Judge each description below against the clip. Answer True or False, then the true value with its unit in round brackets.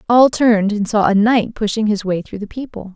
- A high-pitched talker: True (215 Hz)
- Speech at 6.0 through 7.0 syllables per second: False (5.4 syllables/s)